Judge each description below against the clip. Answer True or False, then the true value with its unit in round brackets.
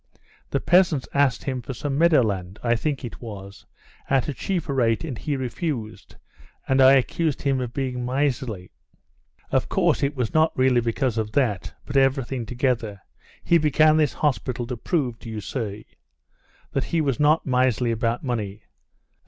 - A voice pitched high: False (130 Hz)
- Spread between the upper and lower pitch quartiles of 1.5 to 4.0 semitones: True (3.6 semitones)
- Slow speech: False (165 wpm)